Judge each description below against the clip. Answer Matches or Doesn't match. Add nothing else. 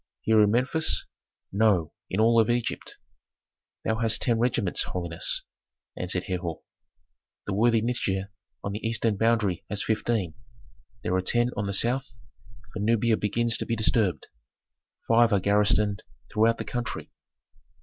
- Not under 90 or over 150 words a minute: Matches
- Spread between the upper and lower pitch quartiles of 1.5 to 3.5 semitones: Matches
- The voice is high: Doesn't match